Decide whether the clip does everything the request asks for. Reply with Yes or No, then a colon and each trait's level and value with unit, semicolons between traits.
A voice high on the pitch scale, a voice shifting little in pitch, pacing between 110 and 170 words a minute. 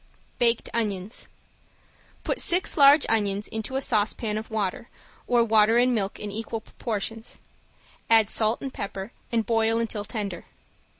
Yes: high, 220 Hz; narrow, 1.9 semitones; average, 140 wpm